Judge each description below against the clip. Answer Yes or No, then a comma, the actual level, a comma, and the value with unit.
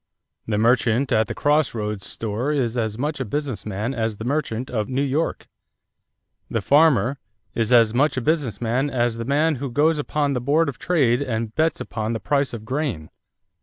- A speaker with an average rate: Yes, average, 195 wpm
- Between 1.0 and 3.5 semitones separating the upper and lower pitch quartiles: No, average, 4.3 semitones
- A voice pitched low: Yes, low, 125 Hz